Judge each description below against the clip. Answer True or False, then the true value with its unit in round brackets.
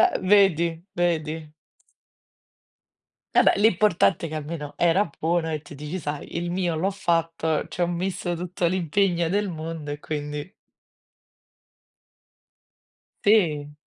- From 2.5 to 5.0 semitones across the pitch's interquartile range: True (2.9 semitones)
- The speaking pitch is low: False (170 Hz)